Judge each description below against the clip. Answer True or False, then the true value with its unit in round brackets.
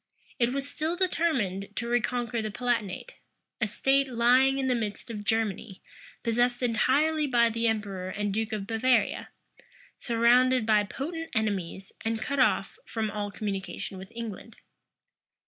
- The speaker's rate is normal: True (145 wpm)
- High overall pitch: True (230 Hz)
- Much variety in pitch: False (3.5 semitones)